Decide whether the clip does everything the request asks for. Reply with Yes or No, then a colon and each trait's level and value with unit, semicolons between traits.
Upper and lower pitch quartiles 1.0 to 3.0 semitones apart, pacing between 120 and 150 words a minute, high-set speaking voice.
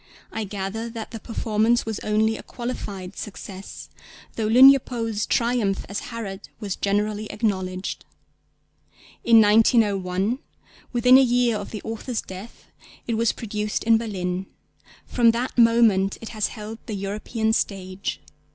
Yes: narrow, 2.6 semitones; slow, 135 wpm; high, 220 Hz